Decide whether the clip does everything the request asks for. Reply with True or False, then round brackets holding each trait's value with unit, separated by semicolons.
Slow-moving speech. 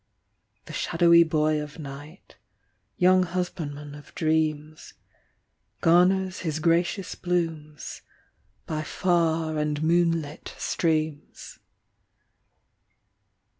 True (80 wpm)